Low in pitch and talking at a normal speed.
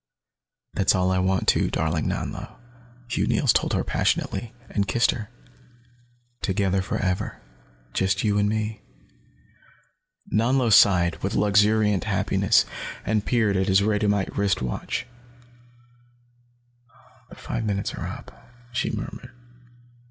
No: low, 100 Hz; slow, 120 wpm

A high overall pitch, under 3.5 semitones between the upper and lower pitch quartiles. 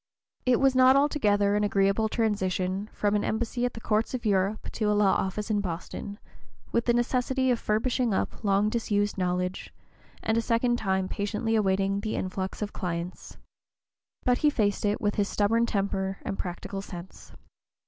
Yes: high, 210 Hz; average, 2.9 semitones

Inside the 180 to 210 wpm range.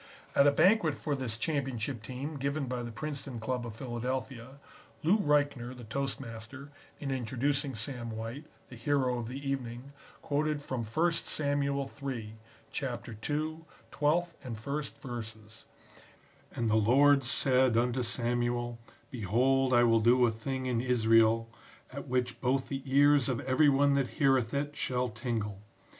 No: average, 150 wpm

